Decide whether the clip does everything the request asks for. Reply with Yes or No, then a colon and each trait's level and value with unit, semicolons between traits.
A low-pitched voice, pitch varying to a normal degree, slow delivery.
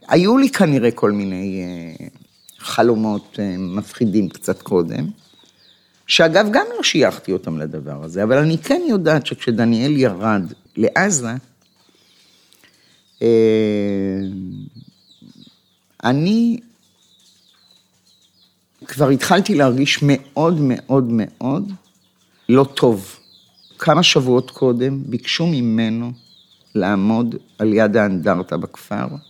No: low, 120 Hz; wide, 5.8 semitones; slow, 85 wpm